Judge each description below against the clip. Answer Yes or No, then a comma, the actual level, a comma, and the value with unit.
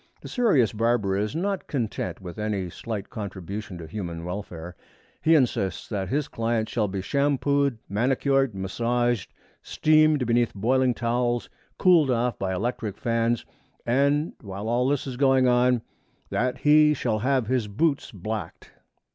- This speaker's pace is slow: No, average, 145 wpm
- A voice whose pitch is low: Yes, low, 120 Hz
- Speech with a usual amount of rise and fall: Yes, average, 4.7 semitones